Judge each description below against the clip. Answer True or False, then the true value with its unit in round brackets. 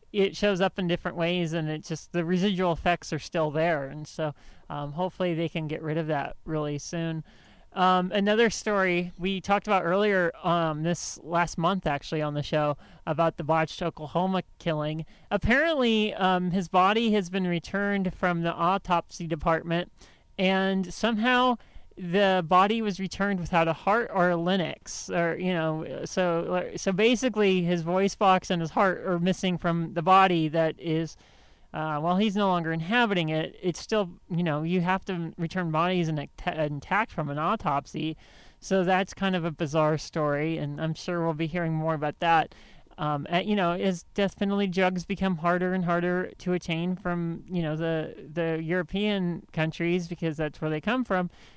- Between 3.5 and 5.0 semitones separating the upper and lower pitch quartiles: False (2.8 semitones)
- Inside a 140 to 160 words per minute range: False (180 wpm)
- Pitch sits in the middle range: True (175 Hz)